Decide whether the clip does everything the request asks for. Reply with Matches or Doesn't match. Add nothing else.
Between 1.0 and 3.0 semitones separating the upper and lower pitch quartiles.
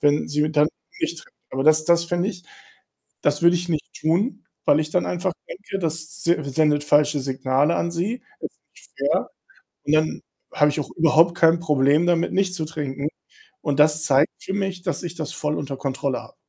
Matches